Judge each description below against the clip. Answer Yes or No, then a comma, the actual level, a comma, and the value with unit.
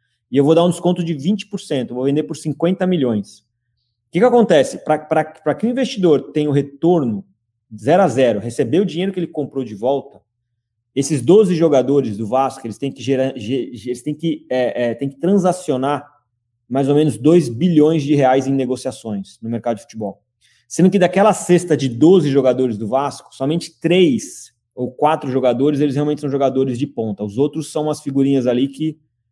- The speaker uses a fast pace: Yes, fast, 190 wpm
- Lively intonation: No, average, 4.6 semitones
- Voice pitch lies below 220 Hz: Yes, medium, 140 Hz